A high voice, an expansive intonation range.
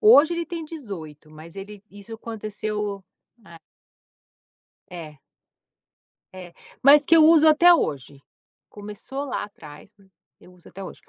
Yes: high, 205 Hz; wide, 8.8 semitones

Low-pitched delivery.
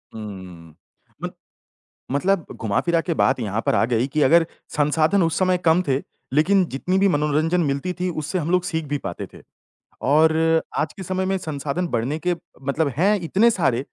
No: medium, 160 Hz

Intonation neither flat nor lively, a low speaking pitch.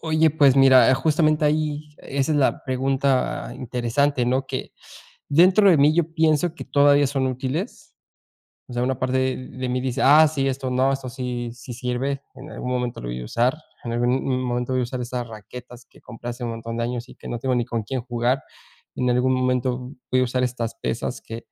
No: narrow, 2.3 semitones; low, 130 Hz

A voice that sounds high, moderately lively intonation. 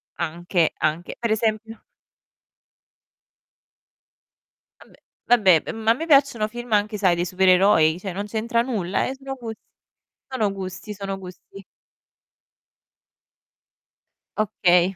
Yes: high, 205 Hz; average, 3.7 semitones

